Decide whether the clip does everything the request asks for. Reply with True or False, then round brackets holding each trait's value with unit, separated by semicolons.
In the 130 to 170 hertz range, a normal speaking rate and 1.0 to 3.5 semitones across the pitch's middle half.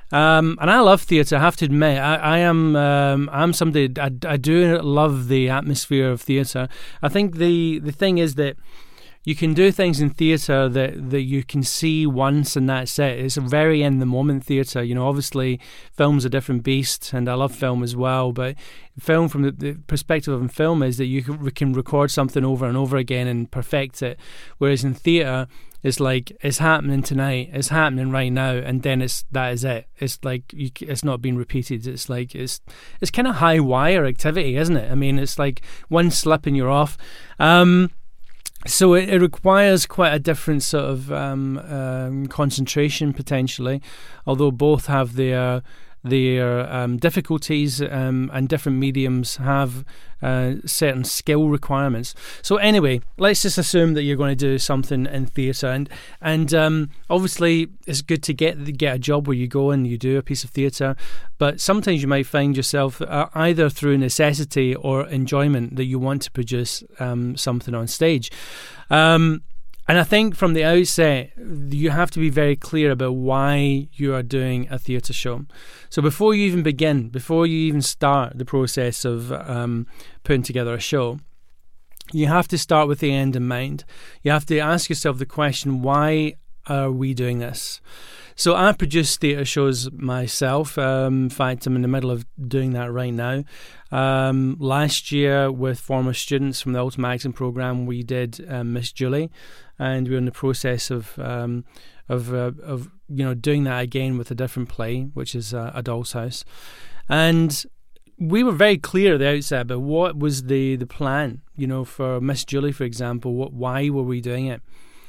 True (140 Hz; 190 wpm; 2.9 semitones)